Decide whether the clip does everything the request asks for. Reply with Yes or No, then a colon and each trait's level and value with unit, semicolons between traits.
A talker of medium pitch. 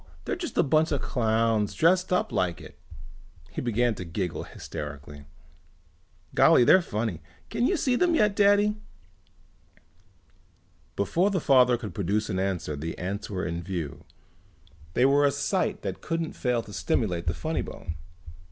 No: low, 115 Hz